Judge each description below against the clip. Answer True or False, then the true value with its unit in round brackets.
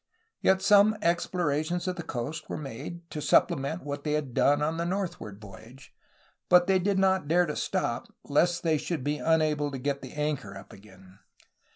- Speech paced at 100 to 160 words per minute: False (185 wpm)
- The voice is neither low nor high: True (155 Hz)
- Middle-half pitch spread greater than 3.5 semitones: True (4.3 semitones)